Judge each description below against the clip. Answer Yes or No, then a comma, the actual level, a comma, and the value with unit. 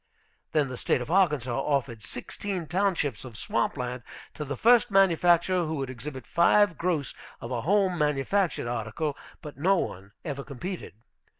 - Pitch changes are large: Yes, wide, 6.2 semitones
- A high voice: No, medium, 150 Hz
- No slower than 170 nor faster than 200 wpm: No, average, 160 wpm